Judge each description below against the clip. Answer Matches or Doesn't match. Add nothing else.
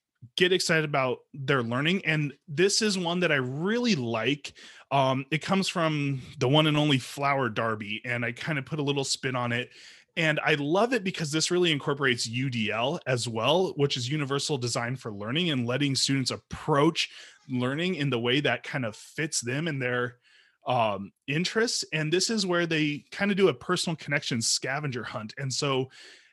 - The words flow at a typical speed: Matches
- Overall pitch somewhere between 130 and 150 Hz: Matches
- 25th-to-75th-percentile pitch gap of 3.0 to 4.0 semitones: Doesn't match